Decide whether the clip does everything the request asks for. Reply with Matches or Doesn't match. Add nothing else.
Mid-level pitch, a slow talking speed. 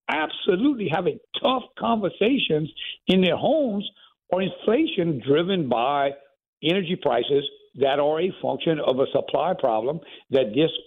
Matches